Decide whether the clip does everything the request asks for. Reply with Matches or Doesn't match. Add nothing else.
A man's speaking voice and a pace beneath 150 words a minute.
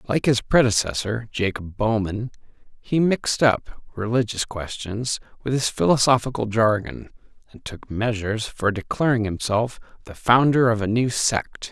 Matches